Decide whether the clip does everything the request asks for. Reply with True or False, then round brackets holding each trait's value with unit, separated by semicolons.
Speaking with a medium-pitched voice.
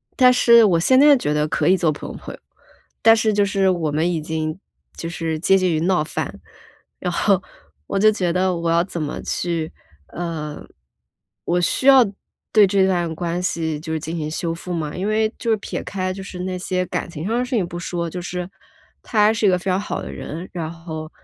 True (175 Hz)